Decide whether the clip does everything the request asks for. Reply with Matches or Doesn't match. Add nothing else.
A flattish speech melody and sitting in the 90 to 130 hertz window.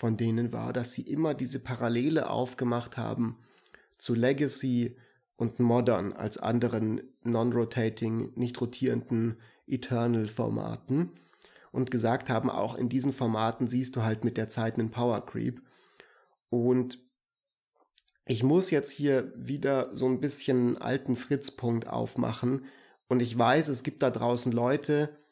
Matches